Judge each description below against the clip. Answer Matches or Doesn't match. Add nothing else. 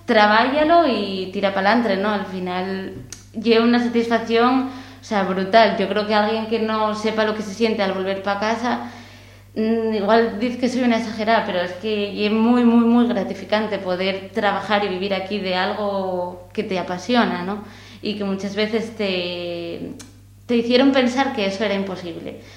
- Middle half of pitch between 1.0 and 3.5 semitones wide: Matches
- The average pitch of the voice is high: Matches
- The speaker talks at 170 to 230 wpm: Matches